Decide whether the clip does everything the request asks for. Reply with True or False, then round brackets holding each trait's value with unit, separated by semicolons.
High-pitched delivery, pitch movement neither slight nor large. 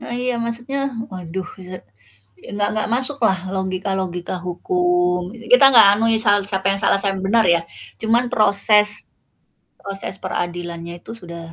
True (195 Hz; 3.8 semitones)